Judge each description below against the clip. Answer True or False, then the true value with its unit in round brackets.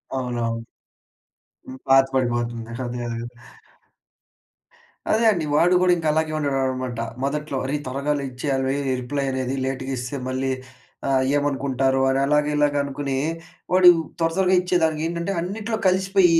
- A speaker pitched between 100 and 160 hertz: True (140 Hz)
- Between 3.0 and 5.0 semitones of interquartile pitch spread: True (3.7 semitones)